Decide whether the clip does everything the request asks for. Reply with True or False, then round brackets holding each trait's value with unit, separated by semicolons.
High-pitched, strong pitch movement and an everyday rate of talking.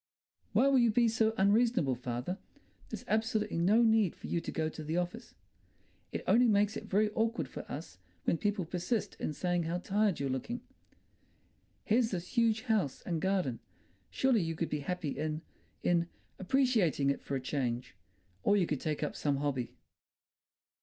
False (180 Hz; 6.2 semitones; 165 wpm)